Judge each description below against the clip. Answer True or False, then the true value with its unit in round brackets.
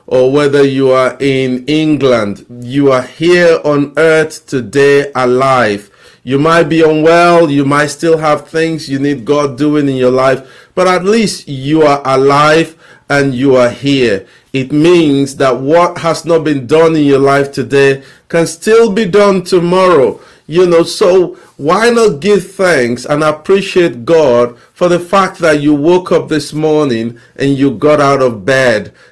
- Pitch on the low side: False (150 Hz)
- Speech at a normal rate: True (165 wpm)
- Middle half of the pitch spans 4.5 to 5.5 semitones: False (3.8 semitones)